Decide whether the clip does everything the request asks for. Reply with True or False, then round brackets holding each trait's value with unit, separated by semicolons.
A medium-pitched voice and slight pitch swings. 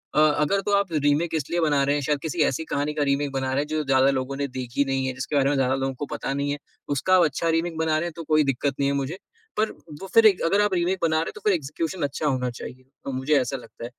False (145 Hz; 3.4 semitones)